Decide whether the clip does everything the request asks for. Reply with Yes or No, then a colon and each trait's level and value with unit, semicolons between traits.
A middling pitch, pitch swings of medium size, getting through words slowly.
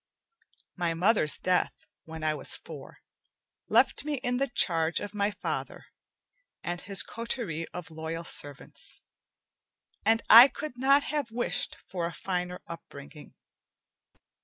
No: medium, 180 Hz; wide, 6.1 semitones; slow, 130 wpm